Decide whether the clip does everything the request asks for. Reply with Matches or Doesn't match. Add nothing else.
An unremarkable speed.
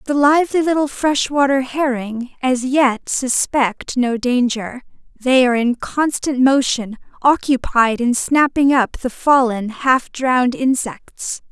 Doesn't match